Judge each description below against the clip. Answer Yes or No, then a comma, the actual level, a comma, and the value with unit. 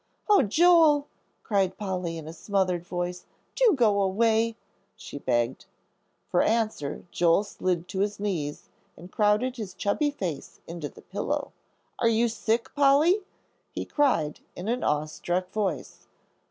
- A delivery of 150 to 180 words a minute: No, average, 140 wpm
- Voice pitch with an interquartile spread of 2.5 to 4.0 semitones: No, average, 4.9 semitones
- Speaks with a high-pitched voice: Yes, high, 200 Hz